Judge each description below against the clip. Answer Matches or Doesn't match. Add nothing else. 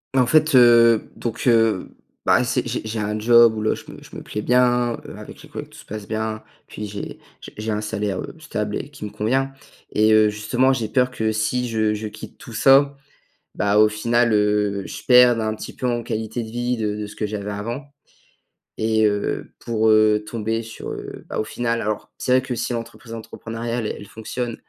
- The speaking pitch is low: Matches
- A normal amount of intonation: Doesn't match